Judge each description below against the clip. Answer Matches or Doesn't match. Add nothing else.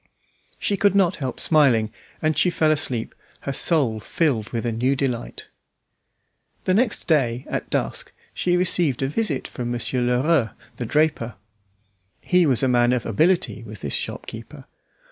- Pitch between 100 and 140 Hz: Matches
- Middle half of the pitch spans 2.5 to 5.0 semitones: Doesn't match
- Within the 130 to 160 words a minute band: Matches